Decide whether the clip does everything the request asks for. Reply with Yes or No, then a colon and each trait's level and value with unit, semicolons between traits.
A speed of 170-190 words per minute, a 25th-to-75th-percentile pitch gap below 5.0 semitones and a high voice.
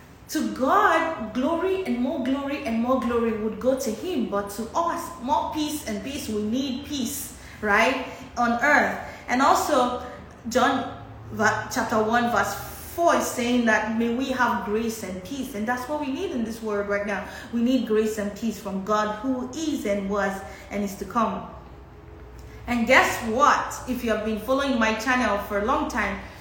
Yes: average, 185 wpm; average, 3.9 semitones; high, 240 Hz